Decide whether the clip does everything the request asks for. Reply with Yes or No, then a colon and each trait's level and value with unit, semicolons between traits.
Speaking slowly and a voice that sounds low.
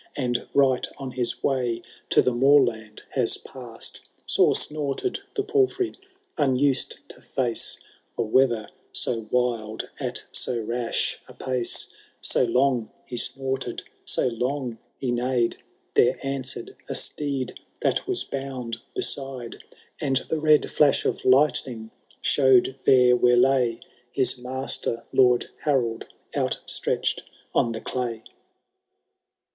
Yes: slow, 120 wpm; low, 125 Hz